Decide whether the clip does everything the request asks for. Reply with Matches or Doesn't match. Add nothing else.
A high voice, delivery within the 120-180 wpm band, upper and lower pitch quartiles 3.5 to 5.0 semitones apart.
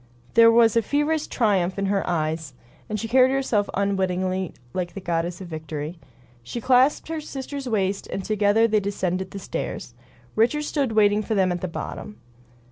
Matches